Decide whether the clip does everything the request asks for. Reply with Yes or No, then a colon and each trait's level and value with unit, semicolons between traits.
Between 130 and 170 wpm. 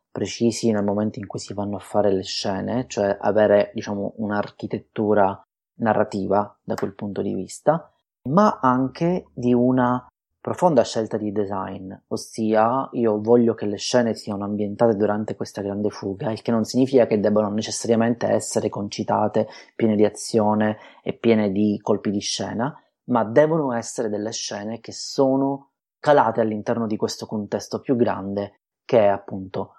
Yes: average, 155 wpm